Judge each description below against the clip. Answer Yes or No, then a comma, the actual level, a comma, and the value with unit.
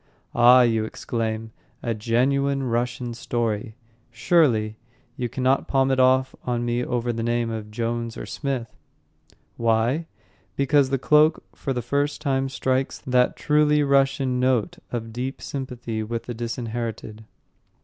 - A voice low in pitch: Yes, low, 125 Hz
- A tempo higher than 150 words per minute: No, average, 140 wpm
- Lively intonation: No, narrow, 2.6 semitones